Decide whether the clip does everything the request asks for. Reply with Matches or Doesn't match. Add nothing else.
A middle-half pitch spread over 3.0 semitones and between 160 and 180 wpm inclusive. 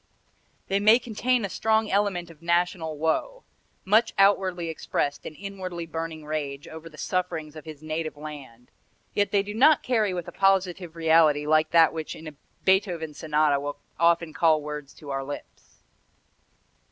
Matches